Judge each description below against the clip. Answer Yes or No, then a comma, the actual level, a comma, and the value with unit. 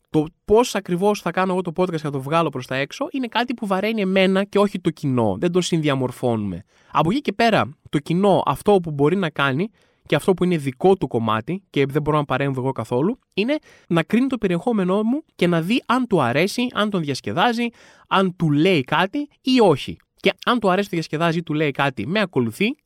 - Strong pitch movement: Yes, wide, 5.8 semitones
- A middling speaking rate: No, fast, 225 wpm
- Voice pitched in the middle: Yes, medium, 180 Hz